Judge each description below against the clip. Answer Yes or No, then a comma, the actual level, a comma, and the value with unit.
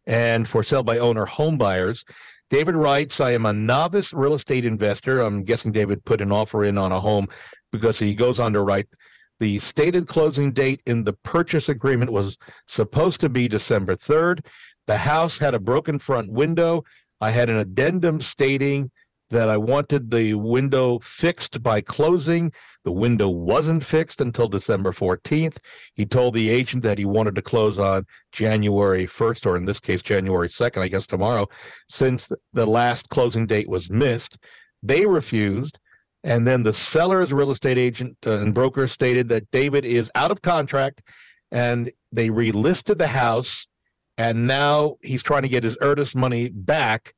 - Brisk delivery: No, average, 170 wpm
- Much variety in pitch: No, average, 4.7 semitones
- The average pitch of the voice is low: Yes, low, 120 Hz